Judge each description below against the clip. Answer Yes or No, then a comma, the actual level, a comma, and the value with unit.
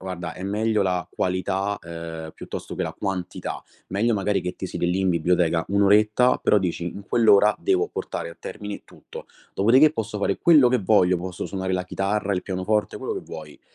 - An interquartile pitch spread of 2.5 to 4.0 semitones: Yes, average, 2.8 semitones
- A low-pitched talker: Yes, very low, 95 Hz